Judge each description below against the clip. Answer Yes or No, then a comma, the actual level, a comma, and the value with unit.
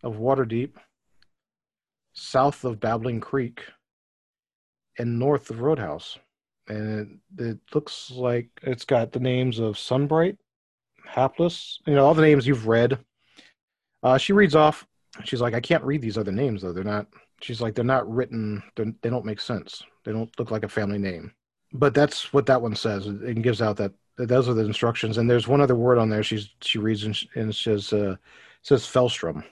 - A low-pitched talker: Yes, low, 120 Hz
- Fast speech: No, average, 195 wpm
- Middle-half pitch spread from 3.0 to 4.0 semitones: Yes, average, 3.4 semitones